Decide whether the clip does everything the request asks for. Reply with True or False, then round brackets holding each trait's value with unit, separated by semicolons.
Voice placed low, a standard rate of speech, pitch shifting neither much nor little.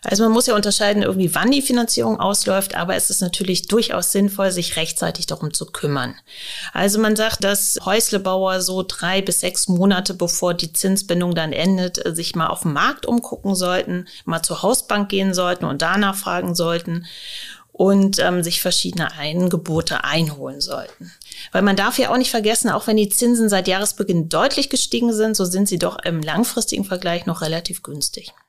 False (190 Hz; 180 wpm; 3.5 semitones)